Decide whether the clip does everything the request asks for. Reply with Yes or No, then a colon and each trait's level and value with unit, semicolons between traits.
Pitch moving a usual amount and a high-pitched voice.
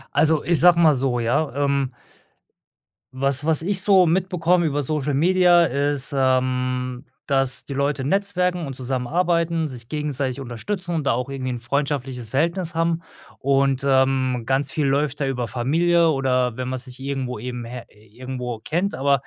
No: average, 4.1 semitones; medium, 140 Hz